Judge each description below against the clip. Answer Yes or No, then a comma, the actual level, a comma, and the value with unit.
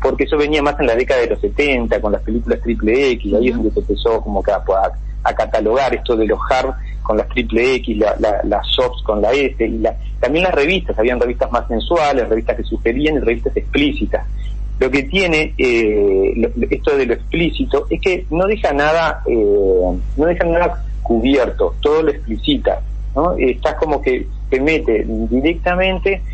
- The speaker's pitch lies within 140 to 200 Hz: Yes, medium, 185 Hz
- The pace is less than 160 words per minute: No, fast, 190 wpm